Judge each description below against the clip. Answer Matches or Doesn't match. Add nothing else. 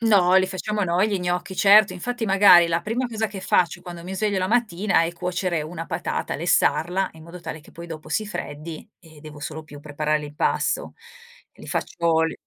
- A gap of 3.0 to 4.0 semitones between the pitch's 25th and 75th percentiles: Matches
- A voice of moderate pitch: Matches